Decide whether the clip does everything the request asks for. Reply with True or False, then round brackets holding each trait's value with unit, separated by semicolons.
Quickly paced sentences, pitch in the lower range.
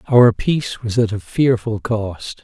False (175 wpm; 115 Hz)